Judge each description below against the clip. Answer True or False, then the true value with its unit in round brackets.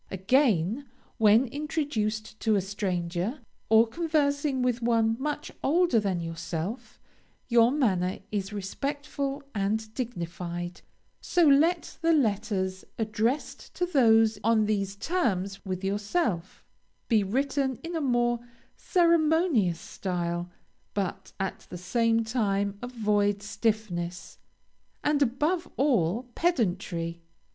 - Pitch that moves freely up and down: True (6.2 semitones)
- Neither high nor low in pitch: False (220 Hz)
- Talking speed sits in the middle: False (110 wpm)